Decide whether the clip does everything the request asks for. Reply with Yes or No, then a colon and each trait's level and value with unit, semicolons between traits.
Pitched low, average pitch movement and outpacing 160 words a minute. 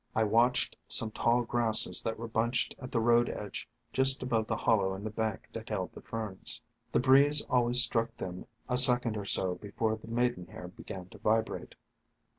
No: low, 115 Hz; narrow, 2.1 semitones; average, 185 wpm